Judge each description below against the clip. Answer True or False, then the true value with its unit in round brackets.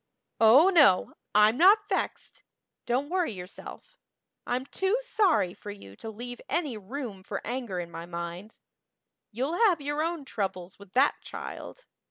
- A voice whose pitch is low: False (245 Hz)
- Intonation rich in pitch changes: True (8.7 semitones)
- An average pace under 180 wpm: True (150 wpm)